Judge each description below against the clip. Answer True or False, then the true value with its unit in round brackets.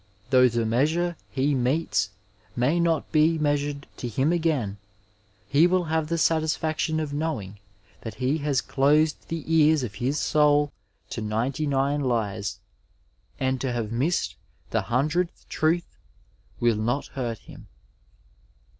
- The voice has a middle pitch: True (145 Hz)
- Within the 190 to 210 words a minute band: False (140 wpm)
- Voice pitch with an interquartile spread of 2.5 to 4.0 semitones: False (4.5 semitones)